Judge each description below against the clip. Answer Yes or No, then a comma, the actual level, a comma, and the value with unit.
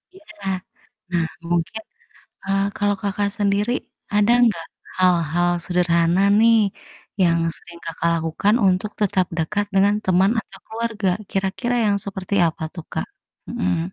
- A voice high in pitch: Yes, high, 195 Hz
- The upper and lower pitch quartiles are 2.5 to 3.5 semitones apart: Yes, average, 2.9 semitones